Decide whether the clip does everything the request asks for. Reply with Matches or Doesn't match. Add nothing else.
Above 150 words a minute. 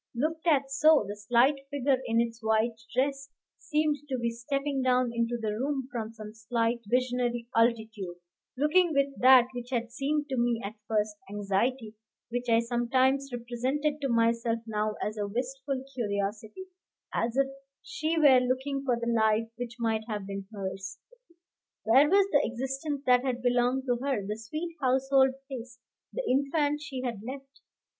Matches